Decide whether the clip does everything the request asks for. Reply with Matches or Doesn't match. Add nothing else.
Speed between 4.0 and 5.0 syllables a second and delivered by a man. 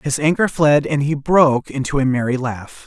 Doesn't match